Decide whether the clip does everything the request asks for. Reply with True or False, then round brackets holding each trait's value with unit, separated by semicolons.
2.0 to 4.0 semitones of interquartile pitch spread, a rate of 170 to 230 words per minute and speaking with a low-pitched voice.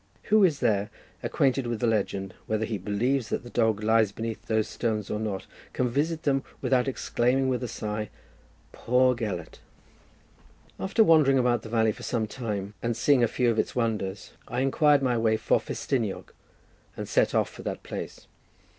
True (3.4 semitones; 180 wpm; 115 Hz)